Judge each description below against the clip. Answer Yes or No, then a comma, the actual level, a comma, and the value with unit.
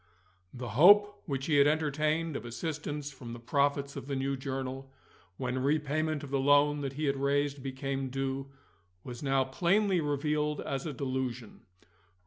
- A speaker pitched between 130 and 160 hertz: Yes, medium, 140 Hz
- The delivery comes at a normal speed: Yes, average, 160 wpm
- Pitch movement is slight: Yes, narrow, 2.1 semitones